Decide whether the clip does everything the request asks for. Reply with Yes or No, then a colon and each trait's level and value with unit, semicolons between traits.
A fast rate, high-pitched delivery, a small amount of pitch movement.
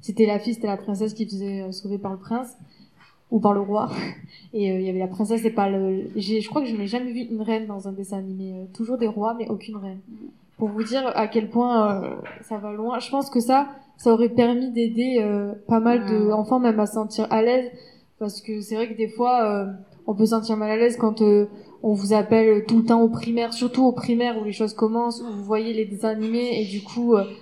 Yes: fast, 255 wpm; high, 220 Hz; narrow, 2.1 semitones